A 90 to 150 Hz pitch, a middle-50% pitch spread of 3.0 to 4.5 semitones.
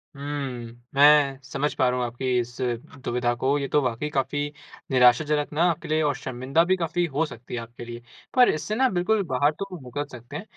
Yes: medium, 140 Hz; average, 3.3 semitones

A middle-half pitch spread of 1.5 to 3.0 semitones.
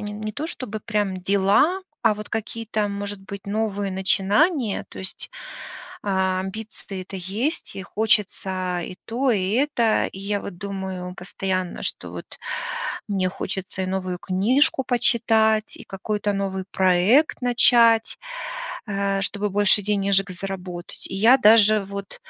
Yes: narrow, 2.6 semitones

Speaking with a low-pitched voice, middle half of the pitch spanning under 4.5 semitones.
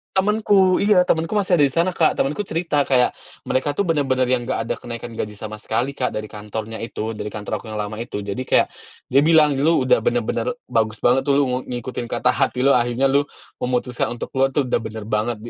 No: low, 125 Hz; average, 4.8 semitones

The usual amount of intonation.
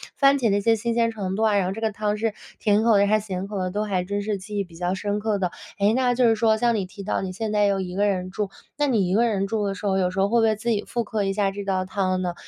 No: narrow, 2.3 semitones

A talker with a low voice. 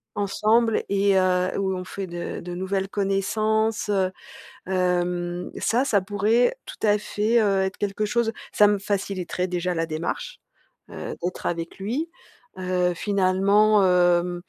No: high, 195 Hz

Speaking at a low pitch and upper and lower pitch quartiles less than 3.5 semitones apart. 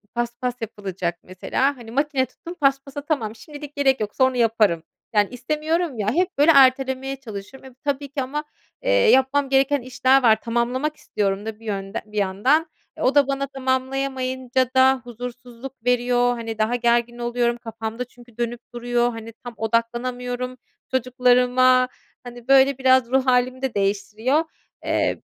No: very high, 250 Hz; narrow, 2.5 semitones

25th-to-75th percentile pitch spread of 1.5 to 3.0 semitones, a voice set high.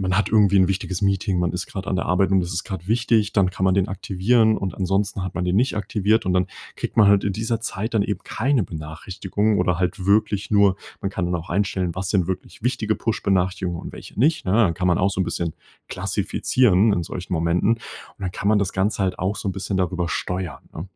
No: narrow, 2.5 semitones; very low, 95 Hz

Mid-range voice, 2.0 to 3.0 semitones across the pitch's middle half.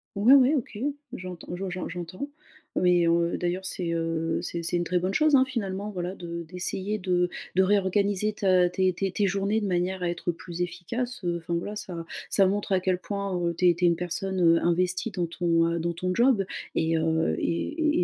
Yes: medium, 180 Hz; narrow, 2.5 semitones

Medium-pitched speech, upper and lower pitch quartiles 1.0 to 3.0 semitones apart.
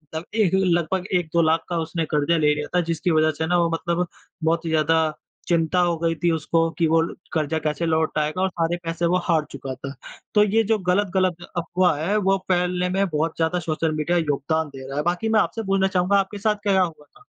Yes: medium, 170 Hz; narrow, 2.6 semitones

